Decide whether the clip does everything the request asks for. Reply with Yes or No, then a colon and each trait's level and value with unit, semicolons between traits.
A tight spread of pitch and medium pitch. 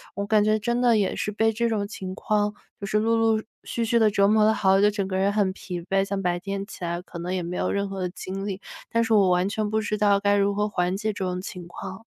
No: narrow, 2.1 semitones; high, 200 Hz